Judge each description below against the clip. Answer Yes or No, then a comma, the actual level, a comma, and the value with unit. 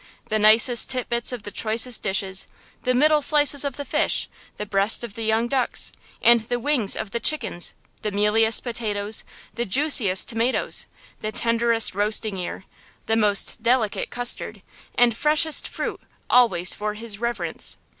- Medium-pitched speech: No, high, 225 Hz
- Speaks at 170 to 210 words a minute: No, average, 155 wpm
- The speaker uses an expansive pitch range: No, average, 2.8 semitones